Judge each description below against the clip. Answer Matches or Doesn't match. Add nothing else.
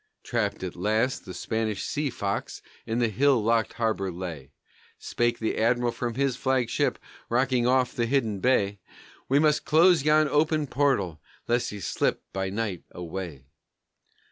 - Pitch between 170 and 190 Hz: Doesn't match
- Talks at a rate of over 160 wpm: Doesn't match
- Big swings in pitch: Doesn't match